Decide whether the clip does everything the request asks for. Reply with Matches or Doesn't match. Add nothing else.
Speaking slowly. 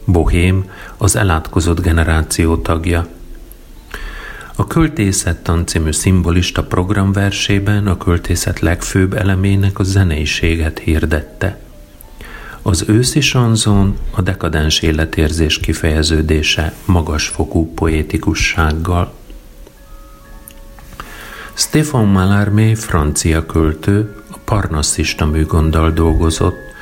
Matches